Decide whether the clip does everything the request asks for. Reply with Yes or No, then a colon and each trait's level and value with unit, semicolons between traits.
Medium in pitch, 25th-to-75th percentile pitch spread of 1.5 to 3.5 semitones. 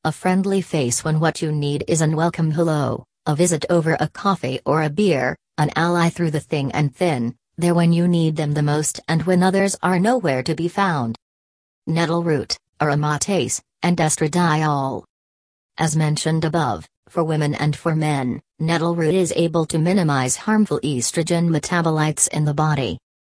Yes: medium, 160 Hz; average, 2.7 semitones